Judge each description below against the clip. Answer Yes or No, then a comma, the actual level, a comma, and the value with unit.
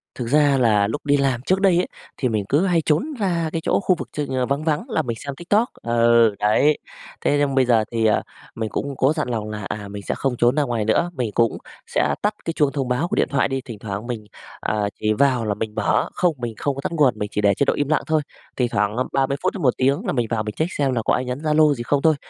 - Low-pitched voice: Yes, low, 130 Hz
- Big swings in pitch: No, average, 4.9 semitones